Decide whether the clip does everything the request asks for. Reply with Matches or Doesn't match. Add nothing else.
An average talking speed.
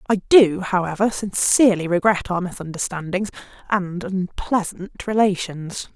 Doesn't match